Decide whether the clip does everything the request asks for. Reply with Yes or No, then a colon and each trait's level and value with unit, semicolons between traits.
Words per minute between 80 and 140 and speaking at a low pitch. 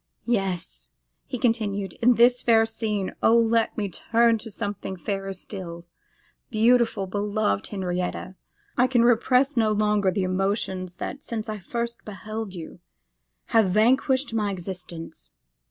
No: slow, 135 wpm; high, 210 Hz